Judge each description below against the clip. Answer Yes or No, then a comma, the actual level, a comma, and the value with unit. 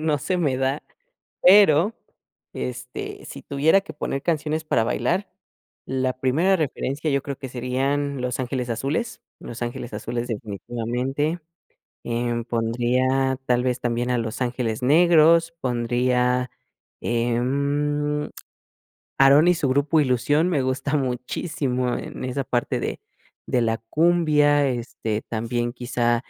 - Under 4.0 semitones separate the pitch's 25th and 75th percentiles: Yes, average, 3.4 semitones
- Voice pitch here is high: No, low, 130 Hz